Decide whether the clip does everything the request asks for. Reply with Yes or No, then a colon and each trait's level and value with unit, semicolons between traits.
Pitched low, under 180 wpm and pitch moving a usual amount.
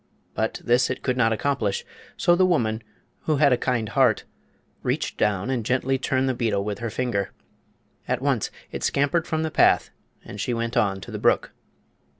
No: low, 125 Hz; average, 185 wpm; average, 3.6 semitones